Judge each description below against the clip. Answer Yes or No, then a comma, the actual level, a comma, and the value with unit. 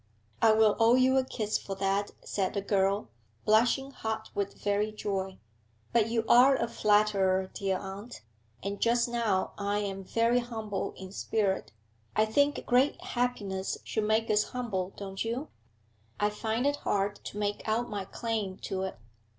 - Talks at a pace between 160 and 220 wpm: Yes, average, 165 wpm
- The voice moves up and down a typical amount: Yes, average, 3.0 semitones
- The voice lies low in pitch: No, high, 210 Hz